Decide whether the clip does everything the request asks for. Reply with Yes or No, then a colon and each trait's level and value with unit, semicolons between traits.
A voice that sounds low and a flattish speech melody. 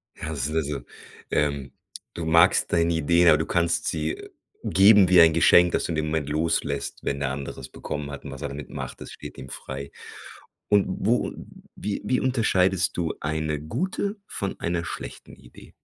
No: very low, 80 Hz; average, 3.5 semitones